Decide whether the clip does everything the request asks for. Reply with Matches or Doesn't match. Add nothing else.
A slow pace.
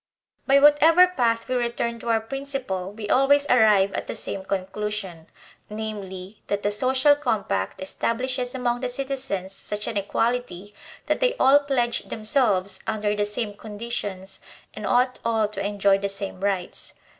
Doesn't match